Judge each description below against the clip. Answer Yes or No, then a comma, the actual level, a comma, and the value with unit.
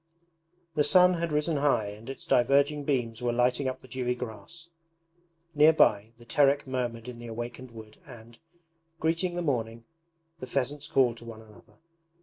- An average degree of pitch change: Yes, average, 4.0 semitones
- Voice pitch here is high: No, low, 125 Hz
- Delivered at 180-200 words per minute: No, average, 165 wpm